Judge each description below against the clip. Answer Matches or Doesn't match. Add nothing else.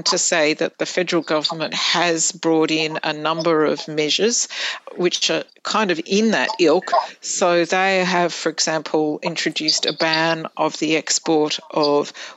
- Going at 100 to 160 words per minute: Matches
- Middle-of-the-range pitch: Matches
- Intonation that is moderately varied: Doesn't match